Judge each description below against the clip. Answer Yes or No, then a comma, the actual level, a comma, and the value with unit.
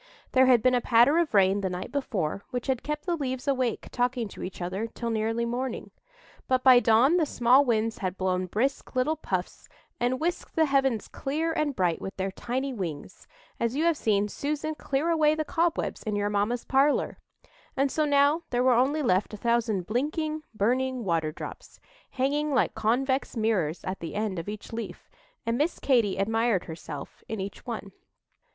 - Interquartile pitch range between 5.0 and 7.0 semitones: Yes, average, 5.3 semitones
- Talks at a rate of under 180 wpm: No, average, 185 wpm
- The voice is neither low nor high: No, high, 240 Hz